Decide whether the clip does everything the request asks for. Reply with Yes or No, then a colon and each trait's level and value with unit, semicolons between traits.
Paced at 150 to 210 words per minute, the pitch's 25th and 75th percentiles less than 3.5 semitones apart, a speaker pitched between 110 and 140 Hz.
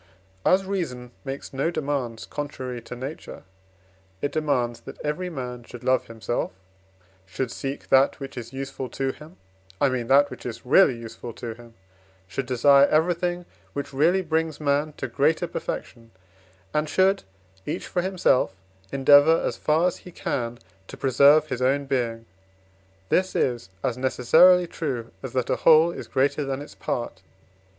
No: average, 160 wpm; average, 4.1 semitones; low, 135 Hz